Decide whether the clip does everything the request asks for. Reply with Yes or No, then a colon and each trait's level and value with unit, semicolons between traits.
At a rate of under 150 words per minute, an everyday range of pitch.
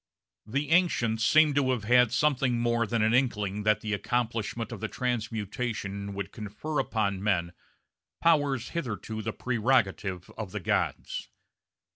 Yes: slow, 135 wpm; average, 3.4 semitones